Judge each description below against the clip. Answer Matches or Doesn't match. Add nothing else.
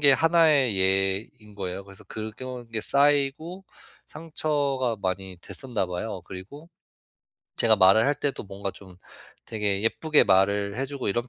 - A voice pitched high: Doesn't match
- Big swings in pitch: Matches